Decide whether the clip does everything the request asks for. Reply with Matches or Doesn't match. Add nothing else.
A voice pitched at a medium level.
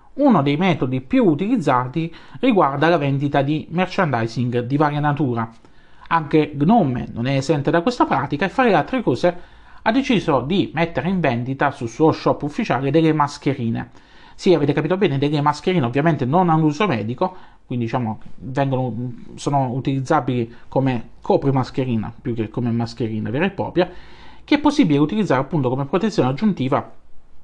Matches